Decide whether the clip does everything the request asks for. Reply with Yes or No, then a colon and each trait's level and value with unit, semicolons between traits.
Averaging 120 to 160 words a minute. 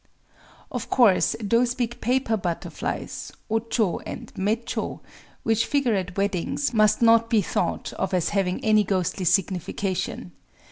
Yes: average, 140 wpm